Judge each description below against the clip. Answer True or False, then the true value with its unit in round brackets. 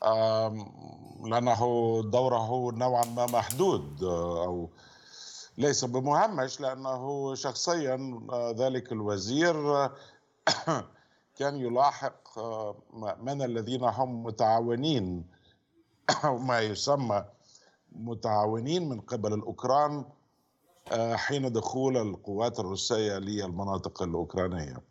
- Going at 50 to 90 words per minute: True (75 wpm)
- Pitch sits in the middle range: False (120 Hz)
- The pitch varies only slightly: False (3.9 semitones)